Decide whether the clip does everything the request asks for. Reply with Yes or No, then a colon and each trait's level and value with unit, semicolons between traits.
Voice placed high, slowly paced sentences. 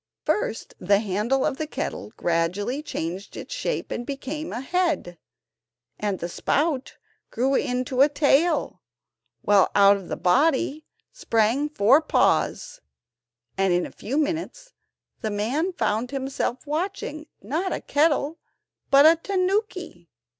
Yes: very high, 275 Hz; slow, 130 wpm